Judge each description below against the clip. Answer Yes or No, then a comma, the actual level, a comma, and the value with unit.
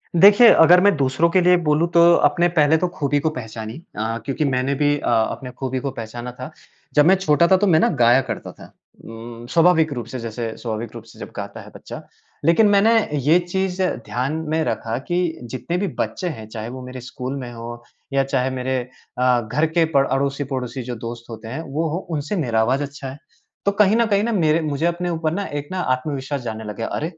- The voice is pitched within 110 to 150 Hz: Yes, medium, 140 Hz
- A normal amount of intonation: No, wide, 5.8 semitones